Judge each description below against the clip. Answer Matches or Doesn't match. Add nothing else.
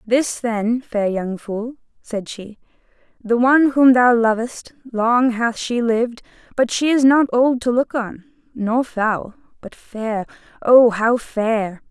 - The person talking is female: Matches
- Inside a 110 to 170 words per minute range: Matches